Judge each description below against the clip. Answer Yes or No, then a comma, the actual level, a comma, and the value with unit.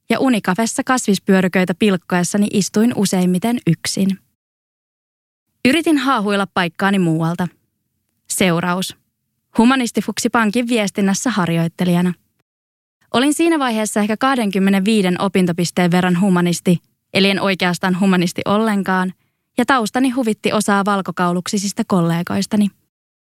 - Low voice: No, high, 195 Hz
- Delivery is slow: Yes, slow, 90 wpm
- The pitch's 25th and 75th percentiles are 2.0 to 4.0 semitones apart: Yes, average, 3.6 semitones